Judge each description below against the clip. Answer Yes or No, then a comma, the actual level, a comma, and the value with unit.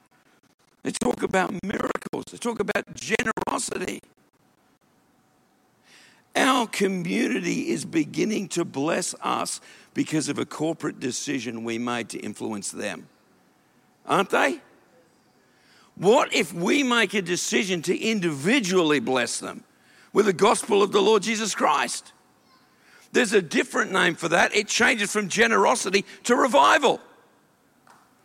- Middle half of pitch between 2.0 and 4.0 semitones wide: No, average, 4.5 semitones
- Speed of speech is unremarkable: No, slow, 120 wpm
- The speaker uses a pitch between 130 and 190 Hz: No, high, 200 Hz